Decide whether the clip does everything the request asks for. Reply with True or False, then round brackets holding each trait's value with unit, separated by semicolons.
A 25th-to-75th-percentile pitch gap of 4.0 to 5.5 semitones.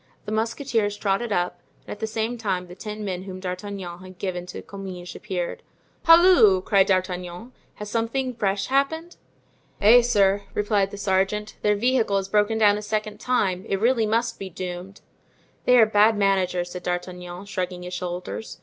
False (3.2 semitones)